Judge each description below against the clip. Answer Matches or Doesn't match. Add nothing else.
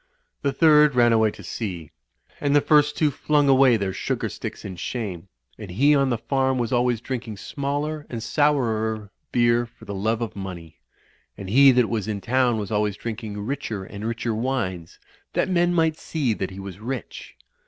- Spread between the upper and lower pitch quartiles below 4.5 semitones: Doesn't match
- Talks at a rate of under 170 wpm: Doesn't match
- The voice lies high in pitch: Doesn't match